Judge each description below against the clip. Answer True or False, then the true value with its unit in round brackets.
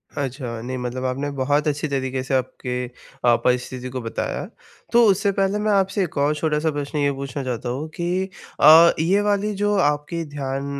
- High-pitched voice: False (145 Hz)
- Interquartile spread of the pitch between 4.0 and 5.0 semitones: True (4.7 semitones)